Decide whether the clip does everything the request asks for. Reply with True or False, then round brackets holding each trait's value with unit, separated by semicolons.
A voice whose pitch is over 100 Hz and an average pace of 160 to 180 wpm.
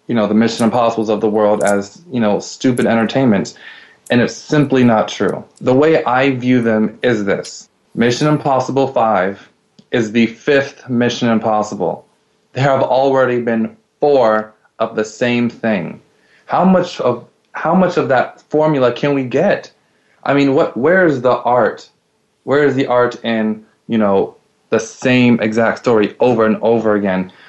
True (120 Hz; 165 wpm)